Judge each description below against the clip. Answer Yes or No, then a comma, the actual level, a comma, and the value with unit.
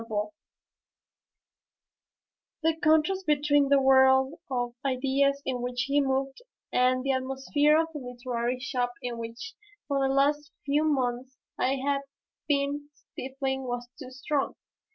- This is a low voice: No, very high, 270 Hz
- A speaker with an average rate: No, slow, 130 wpm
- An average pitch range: No, narrow, 2.2 semitones